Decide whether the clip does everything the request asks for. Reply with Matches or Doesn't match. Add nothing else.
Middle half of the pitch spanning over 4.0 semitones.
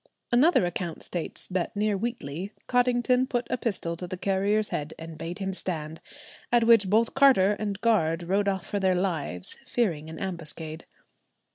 Matches